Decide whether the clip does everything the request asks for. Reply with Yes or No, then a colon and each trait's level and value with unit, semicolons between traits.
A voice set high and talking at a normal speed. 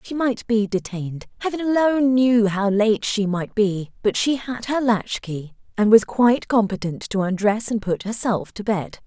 Yes: high, 215 Hz; average, 190 wpm